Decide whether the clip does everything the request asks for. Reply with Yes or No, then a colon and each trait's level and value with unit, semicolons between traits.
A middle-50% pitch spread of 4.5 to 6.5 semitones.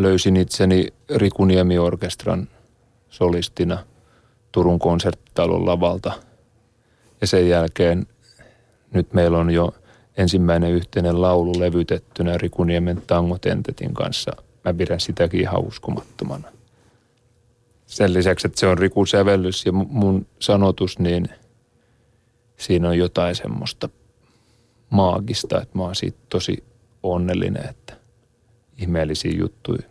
Yes: average, 4.9 semitones